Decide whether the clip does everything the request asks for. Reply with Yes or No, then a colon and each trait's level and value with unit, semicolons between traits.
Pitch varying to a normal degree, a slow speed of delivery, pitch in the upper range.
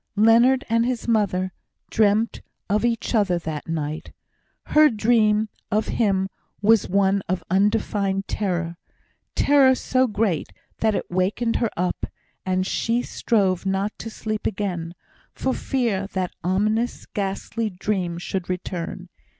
Yes: average, 3.5 semitones; slow, 130 wpm; high, 205 Hz